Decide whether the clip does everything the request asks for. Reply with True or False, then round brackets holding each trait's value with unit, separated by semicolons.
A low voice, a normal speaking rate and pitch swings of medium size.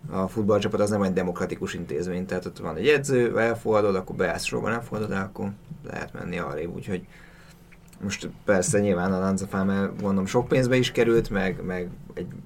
False (100 Hz; 165 wpm; 3.1 semitones)